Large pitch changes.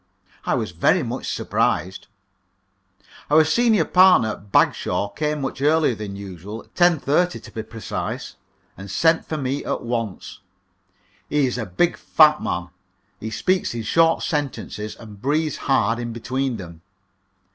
Yes: wide, 6.6 semitones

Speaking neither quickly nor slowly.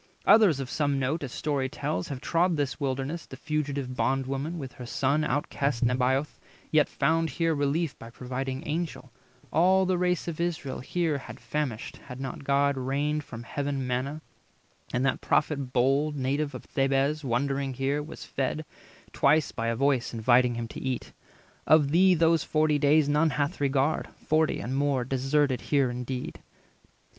Yes: average, 170 wpm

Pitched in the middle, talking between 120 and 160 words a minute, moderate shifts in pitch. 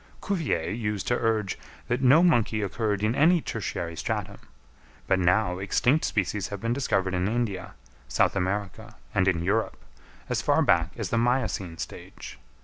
No: low, 105 Hz; average, 155 wpm; average, 4.2 semitones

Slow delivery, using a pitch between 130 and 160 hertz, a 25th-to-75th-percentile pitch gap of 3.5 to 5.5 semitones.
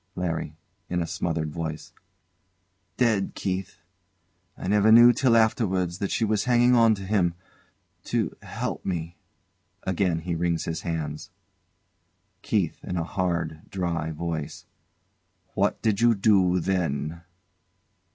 No: slow, 130 wpm; very low, 90 Hz; average, 3.9 semitones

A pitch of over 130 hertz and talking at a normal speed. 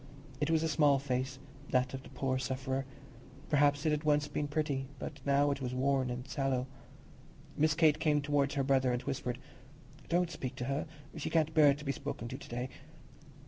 Yes: medium, 140 Hz; average, 195 wpm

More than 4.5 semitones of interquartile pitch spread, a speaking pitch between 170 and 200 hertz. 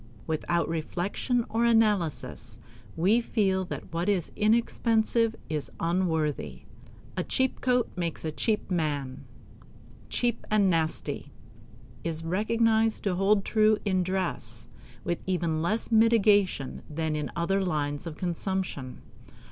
Yes: average, 5.1 semitones; medium, 185 Hz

